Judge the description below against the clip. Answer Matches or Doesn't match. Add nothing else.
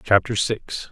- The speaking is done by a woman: Doesn't match